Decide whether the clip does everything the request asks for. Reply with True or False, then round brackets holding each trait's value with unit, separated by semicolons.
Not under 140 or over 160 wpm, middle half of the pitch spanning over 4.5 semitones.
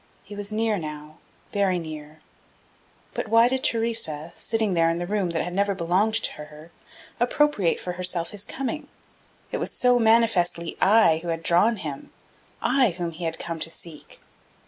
False (170 wpm; 5.2 semitones)